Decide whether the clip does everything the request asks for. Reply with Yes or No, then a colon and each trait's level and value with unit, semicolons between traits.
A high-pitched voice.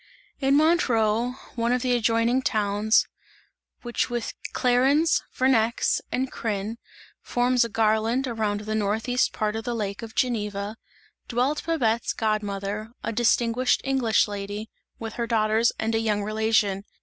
Yes: high, 225 Hz